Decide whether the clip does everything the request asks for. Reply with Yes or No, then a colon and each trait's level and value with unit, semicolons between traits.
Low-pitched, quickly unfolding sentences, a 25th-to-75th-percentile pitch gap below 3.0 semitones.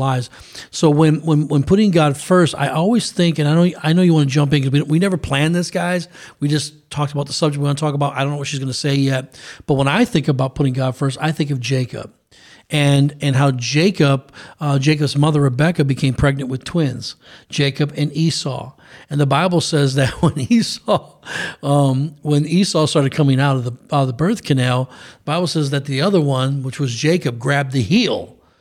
No: medium, 145 Hz; fast, 225 wpm; narrow, 2.5 semitones